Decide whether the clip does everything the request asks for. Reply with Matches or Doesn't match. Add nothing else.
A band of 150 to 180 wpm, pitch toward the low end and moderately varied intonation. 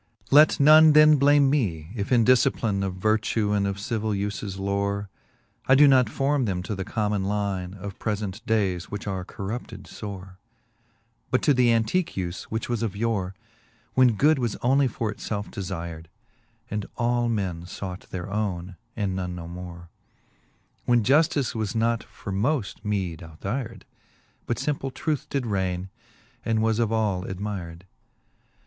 Matches